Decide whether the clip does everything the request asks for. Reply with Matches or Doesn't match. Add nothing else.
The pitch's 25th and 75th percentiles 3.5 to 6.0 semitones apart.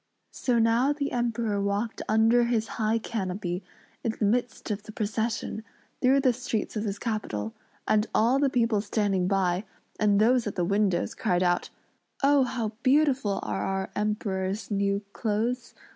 Doesn't match